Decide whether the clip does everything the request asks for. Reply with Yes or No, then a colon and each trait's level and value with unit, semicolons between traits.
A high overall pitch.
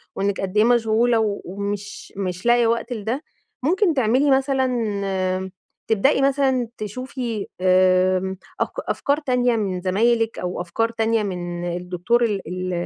Yes: high, 220 Hz